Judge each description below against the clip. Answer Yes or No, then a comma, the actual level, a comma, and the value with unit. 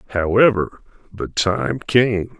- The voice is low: Yes, low, 105 Hz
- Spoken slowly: Yes, slow, 100 wpm